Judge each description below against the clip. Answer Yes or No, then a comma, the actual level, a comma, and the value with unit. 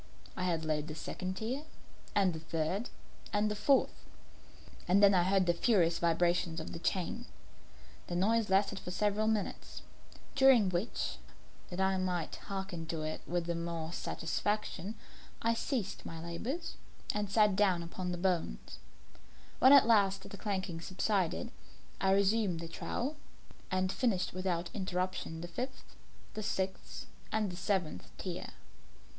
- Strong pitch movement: No, average, 3.4 semitones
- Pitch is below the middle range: No, high, 190 Hz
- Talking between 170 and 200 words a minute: No, average, 145 wpm